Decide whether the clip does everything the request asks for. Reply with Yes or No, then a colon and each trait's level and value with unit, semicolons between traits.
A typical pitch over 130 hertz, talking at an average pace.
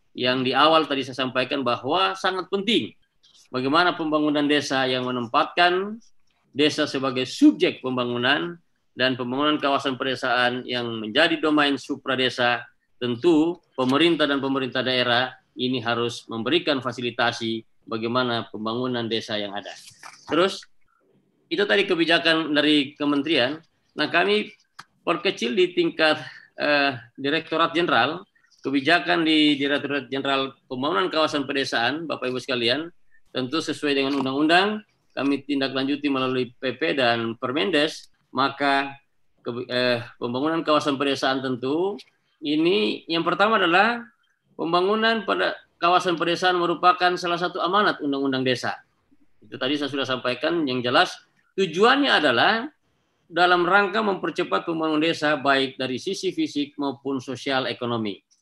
Yes: medium, 140 Hz; average, 120 wpm